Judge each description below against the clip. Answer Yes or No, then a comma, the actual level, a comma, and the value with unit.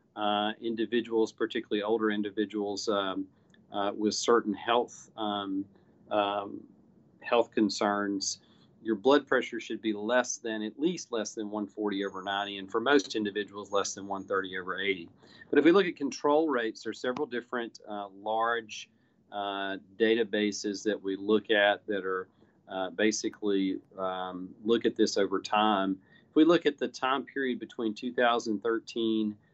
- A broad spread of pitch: No, narrow, 2.4 semitones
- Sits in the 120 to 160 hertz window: No, low, 105 Hz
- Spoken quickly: No, average, 150 wpm